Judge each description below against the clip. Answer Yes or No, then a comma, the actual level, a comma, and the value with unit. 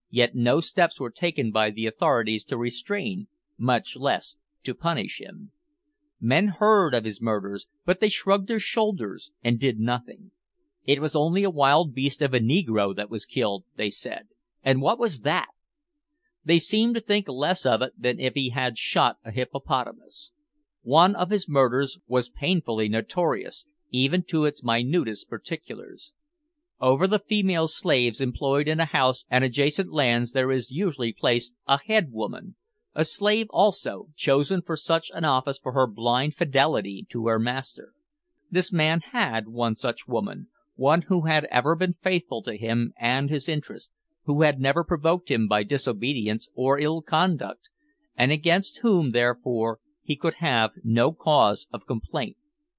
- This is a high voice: No, medium, 150 Hz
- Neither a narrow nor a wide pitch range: No, wide, 8.0 semitones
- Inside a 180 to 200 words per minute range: No, average, 165 wpm